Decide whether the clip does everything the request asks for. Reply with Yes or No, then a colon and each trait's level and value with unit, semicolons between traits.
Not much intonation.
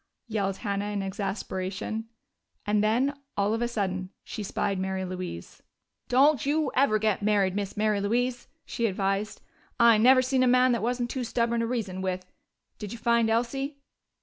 No: average, 3.6 semitones